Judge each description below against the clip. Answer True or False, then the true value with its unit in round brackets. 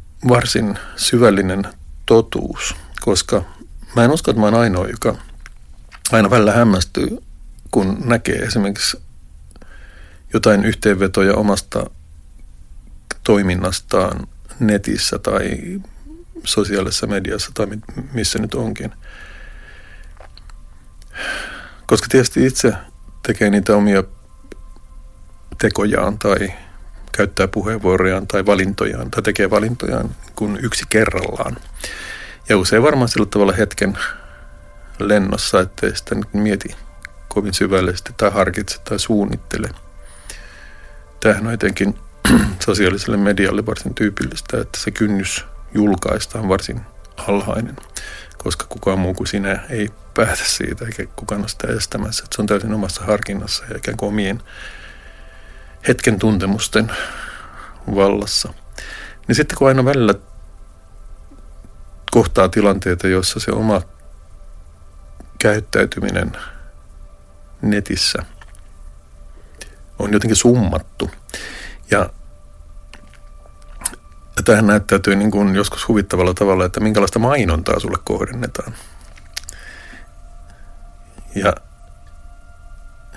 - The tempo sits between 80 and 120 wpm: True (95 wpm)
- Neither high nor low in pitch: False (100 Hz)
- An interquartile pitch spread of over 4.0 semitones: True (5.5 semitones)